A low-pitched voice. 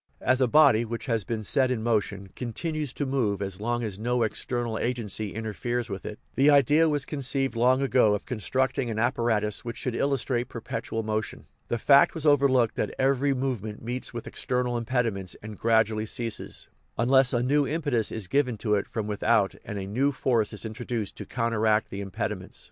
Yes: low, 120 Hz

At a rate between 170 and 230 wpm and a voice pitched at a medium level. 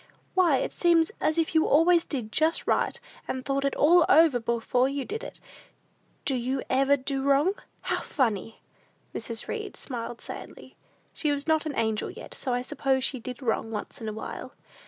No: average, 185 wpm; very high, 275 Hz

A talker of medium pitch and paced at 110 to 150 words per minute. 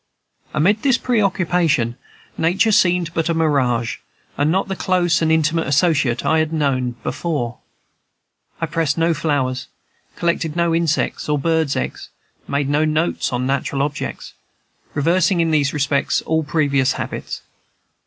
Yes: medium, 160 Hz; average, 140 wpm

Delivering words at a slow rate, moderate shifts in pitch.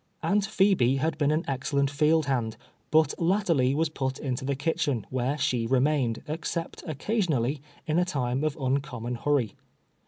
No: average, 155 wpm; average, 3.4 semitones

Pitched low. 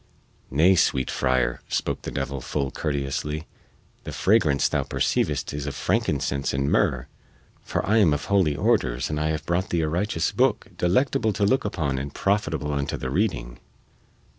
Yes: very low, 75 Hz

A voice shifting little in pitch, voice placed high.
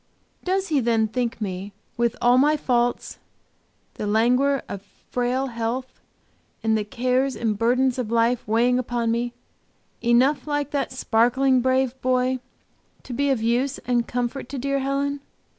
Yes: narrow, 2.3 semitones; very high, 250 Hz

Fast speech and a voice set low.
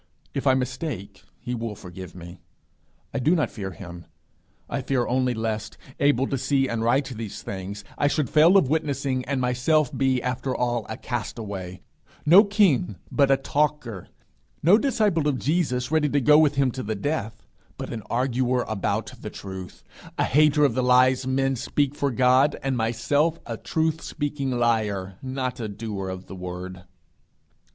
No: average, 170 wpm; low, 130 Hz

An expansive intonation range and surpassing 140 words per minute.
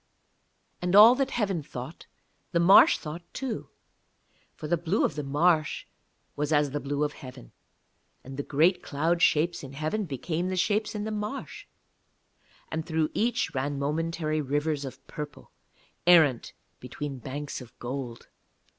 No: average, 3.9 semitones; average, 150 wpm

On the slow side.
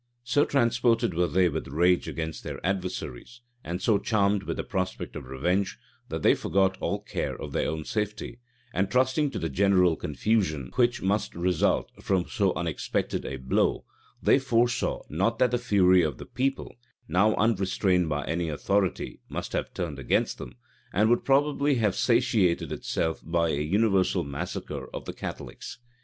No: average, 165 wpm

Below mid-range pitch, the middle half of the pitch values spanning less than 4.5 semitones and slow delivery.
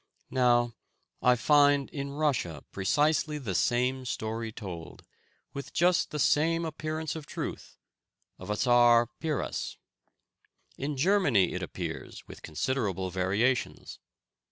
No: low, 130 Hz; average, 5.0 semitones; slow, 115 wpm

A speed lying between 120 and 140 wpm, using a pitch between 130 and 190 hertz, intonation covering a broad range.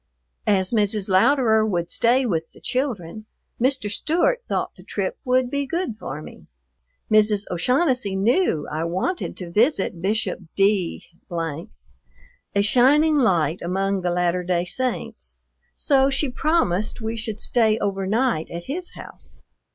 No: slow, 135 wpm; high, 215 Hz; wide, 6.4 semitones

